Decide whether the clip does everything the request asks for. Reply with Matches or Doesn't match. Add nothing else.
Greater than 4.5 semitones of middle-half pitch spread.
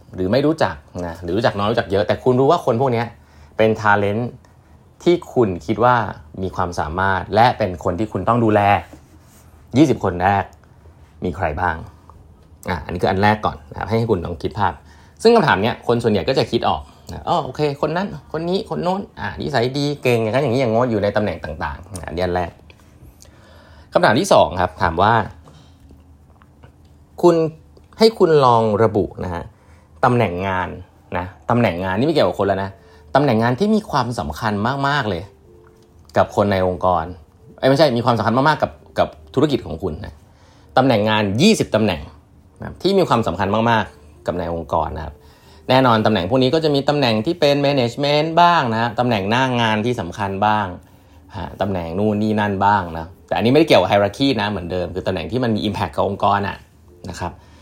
Matches